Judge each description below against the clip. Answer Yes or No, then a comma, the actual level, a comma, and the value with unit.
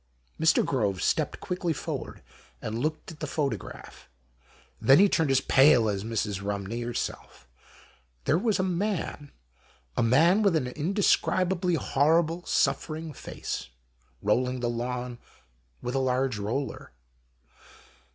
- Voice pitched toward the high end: No, low, 135 Hz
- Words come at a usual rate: No, slow, 130 wpm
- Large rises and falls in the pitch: Yes, wide, 5.7 semitones